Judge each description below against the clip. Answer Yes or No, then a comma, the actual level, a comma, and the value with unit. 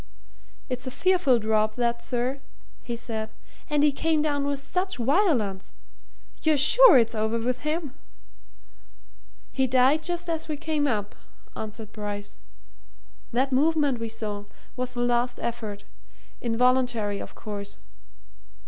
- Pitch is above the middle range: Yes, very high, 250 Hz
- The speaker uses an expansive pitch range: No, average, 5.0 semitones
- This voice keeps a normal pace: No, slow, 130 wpm